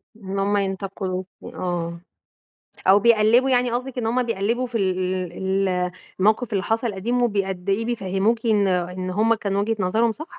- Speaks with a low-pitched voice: No, high, 205 Hz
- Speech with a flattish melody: No, average, 3.4 semitones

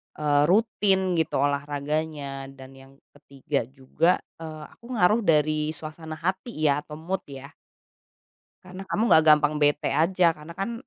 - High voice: No, medium, 155 Hz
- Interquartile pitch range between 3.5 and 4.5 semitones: Yes, average, 4.0 semitones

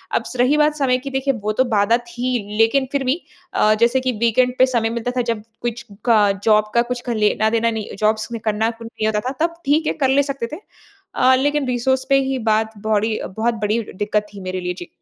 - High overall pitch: Yes, high, 235 Hz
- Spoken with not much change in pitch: No, average, 3.2 semitones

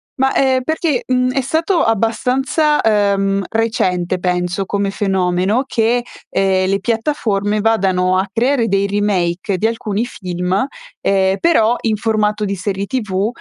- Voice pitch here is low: No, high, 210 Hz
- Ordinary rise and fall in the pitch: Yes, average, 3.8 semitones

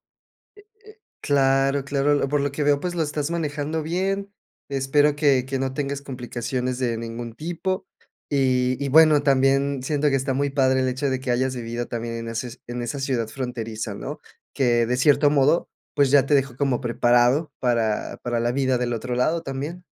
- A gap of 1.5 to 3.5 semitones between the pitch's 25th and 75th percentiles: Yes, average, 2.8 semitones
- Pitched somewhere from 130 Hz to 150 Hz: Yes, low, 135 Hz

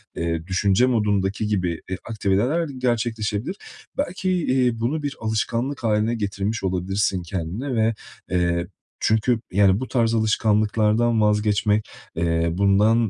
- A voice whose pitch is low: Yes, low, 105 Hz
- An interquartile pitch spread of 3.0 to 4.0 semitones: Yes, average, 3.4 semitones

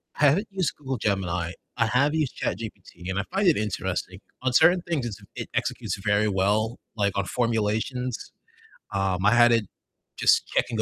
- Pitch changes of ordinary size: Yes, average, 4.6 semitones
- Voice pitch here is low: Yes, low, 110 Hz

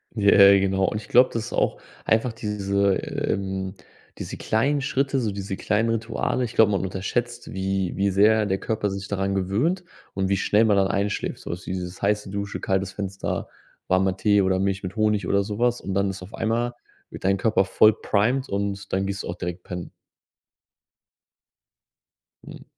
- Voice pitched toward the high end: No, low, 100 Hz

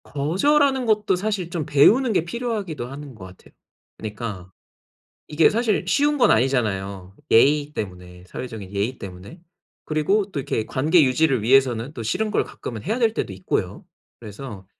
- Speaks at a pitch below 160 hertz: Yes, medium, 140 Hz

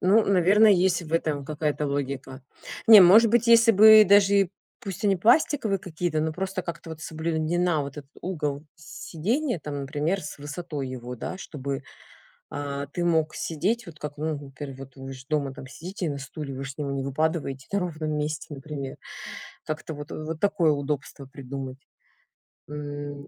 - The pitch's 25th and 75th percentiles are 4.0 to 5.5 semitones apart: Yes, average, 4.4 semitones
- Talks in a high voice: No, medium, 155 Hz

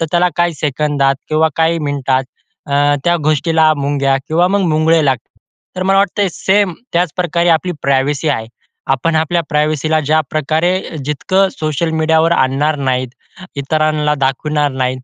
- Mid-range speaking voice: Yes, medium, 155 Hz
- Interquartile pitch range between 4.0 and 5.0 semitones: No, average, 2.9 semitones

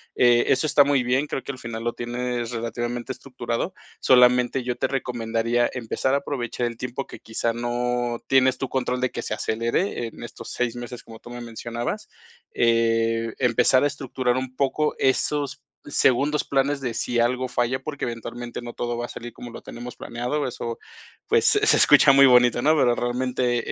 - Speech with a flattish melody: Yes, narrow, 1.7 semitones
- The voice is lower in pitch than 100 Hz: No, low, 120 Hz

